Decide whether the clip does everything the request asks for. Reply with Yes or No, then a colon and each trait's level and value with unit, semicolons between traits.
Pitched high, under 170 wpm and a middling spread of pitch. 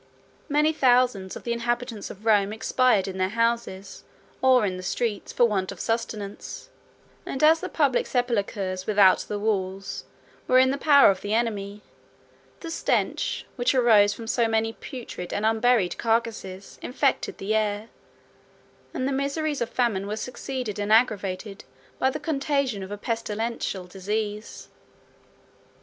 Yes: high, 225 Hz; average, 150 wpm; average, 3.7 semitones